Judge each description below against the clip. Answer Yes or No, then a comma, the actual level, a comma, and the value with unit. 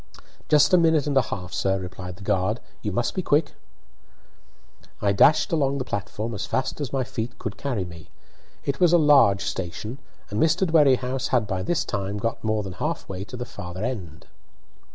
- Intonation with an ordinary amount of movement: No, wide, 6.2 semitones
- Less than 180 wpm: No, average, 195 wpm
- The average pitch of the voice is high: No, low, 115 Hz